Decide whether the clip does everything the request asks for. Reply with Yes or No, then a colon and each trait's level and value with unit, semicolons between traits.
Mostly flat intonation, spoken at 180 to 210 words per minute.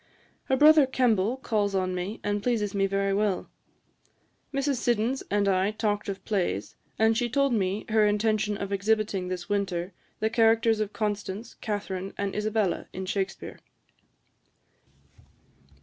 No: narrow, 2.3 semitones; average, 140 wpm